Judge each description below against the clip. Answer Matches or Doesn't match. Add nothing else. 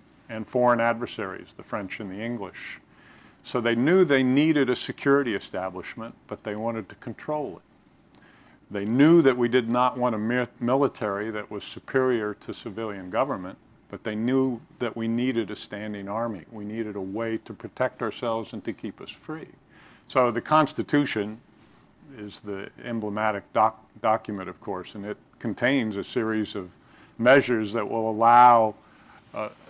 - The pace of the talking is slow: Doesn't match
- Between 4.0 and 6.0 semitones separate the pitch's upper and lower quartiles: Doesn't match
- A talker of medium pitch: Doesn't match